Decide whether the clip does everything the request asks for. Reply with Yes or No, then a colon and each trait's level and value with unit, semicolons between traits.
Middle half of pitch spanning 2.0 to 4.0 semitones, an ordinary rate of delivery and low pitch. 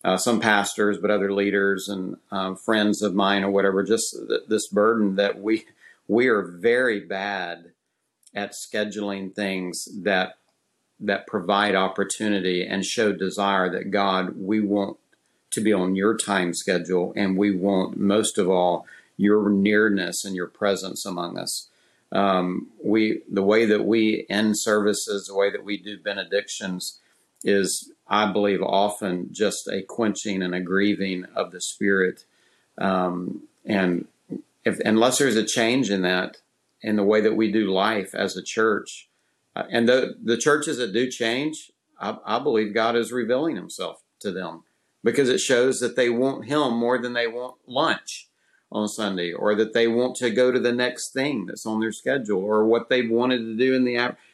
Yes: narrow, 2.5 semitones; average, 170 wpm; low, 105 Hz